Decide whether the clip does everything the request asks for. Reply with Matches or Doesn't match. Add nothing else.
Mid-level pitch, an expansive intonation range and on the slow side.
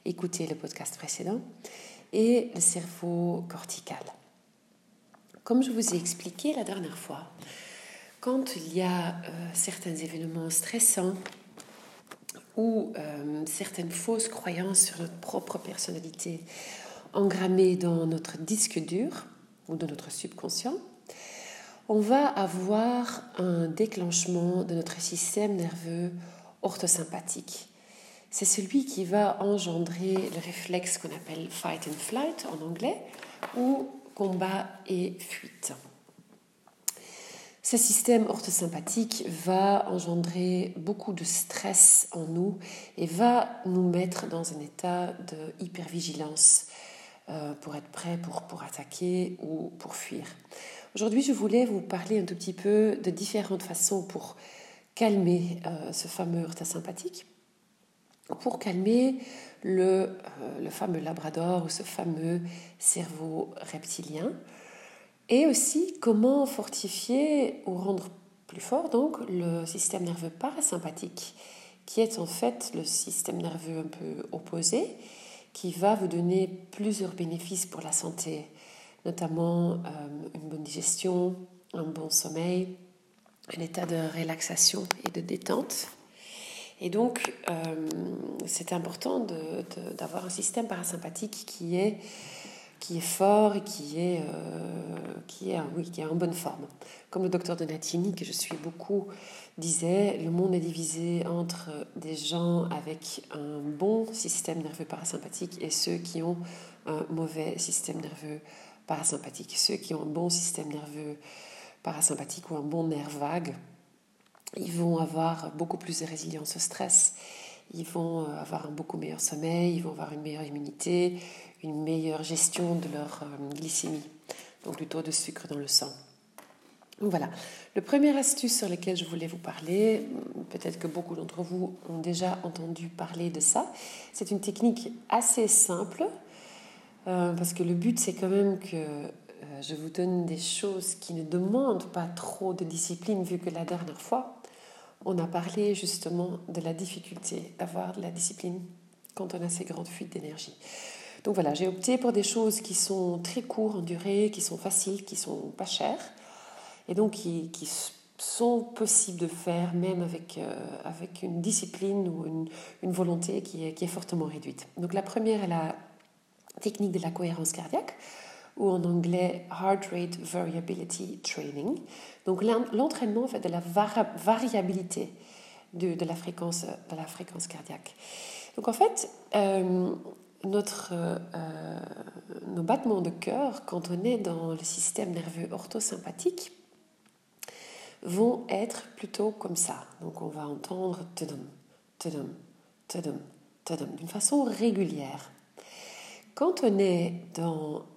Doesn't match